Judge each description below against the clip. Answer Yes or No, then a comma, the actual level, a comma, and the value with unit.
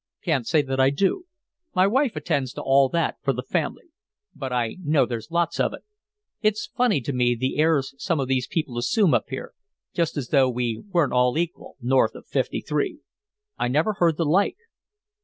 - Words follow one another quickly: No, average, 195 wpm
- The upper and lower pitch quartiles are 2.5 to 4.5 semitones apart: No, average, 5.1 semitones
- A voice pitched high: No, medium, 145 Hz